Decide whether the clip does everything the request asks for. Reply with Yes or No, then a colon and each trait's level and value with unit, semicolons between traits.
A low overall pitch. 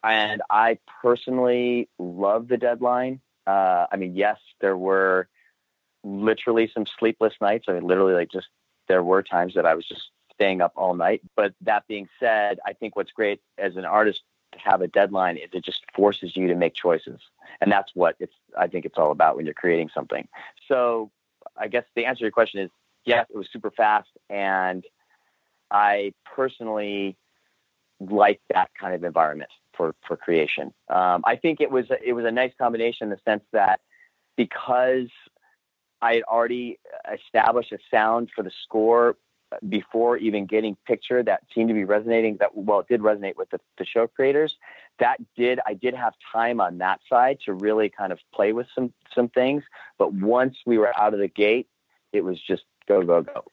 Yes: low, 110 Hz